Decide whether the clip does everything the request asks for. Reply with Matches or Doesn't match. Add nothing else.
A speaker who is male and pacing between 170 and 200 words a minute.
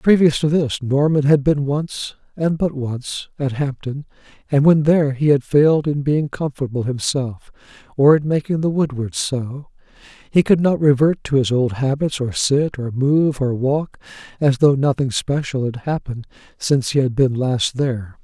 Matches